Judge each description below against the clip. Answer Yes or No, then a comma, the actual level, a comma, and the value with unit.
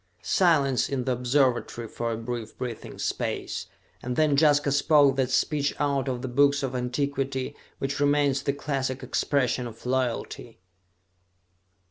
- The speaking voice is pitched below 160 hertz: Yes, low, 135 Hz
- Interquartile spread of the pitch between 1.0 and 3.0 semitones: Yes, narrow, 2.4 semitones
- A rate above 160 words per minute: No, average, 140 wpm